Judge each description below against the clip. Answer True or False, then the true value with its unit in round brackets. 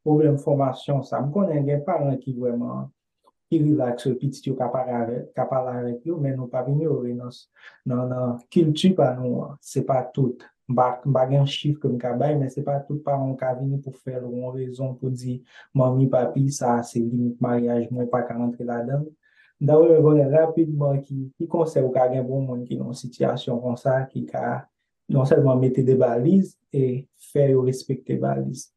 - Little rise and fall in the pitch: True (2.3 semitones)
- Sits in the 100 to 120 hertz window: False (130 Hz)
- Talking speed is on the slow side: False (190 wpm)